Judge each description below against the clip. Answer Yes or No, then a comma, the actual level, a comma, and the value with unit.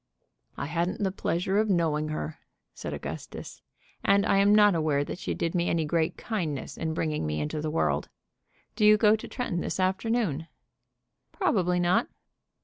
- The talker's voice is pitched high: No, medium, 175 Hz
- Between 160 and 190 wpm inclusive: Yes, average, 170 wpm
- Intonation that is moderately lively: Yes, average, 4.6 semitones